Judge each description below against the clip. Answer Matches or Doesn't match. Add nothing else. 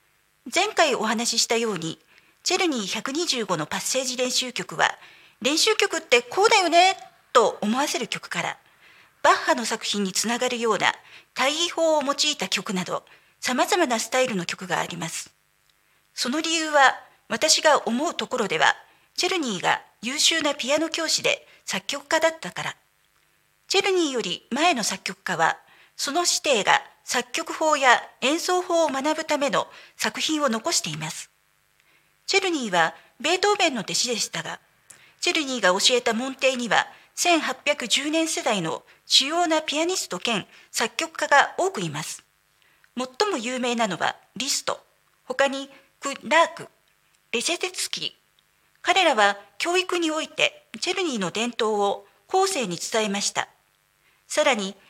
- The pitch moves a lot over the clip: Matches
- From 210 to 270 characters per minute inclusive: Doesn't match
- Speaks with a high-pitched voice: Matches